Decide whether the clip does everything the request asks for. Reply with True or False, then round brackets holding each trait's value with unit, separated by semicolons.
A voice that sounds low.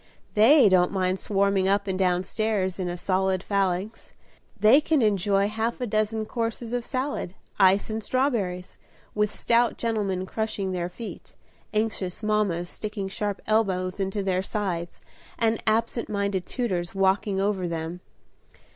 False (200 Hz)